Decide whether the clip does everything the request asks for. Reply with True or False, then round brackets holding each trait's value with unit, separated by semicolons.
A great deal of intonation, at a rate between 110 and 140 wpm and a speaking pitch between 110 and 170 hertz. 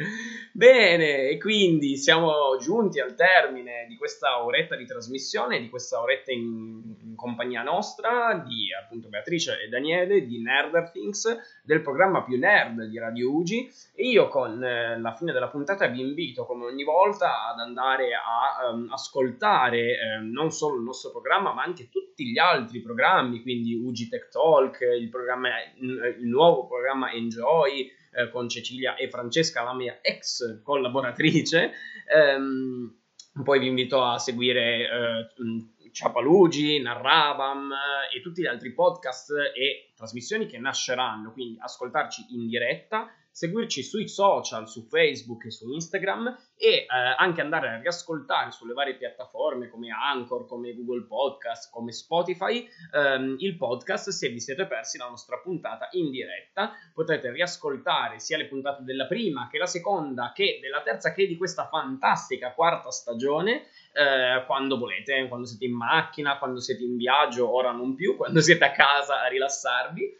False (6.3 semitones; 155 wpm; 135 Hz)